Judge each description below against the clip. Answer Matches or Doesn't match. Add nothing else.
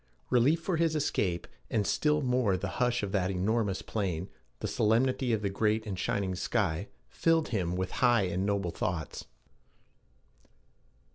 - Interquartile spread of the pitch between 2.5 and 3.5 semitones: Doesn't match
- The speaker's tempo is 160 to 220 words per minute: Doesn't match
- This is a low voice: Matches